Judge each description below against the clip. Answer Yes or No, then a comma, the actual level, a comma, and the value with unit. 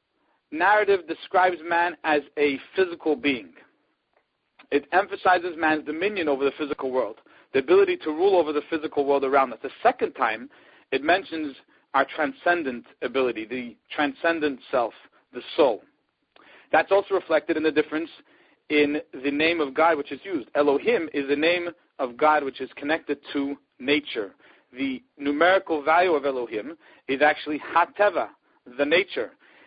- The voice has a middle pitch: Yes, medium, 155 Hz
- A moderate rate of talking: Yes, average, 150 wpm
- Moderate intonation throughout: Yes, average, 3.5 semitones